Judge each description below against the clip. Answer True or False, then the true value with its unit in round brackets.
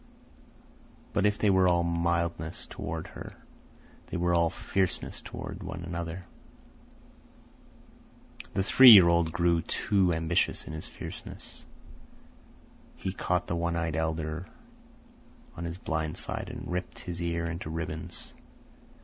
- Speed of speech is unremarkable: False (130 wpm)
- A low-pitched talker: True (85 Hz)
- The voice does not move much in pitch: True (1.7 semitones)